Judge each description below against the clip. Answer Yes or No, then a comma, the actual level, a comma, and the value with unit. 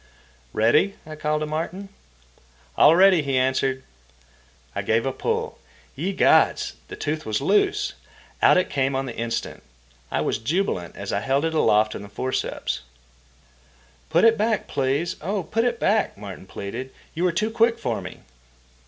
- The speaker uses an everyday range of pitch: No, wide, 8.2 semitones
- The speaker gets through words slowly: No, average, 165 wpm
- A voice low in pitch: No, medium, 145 Hz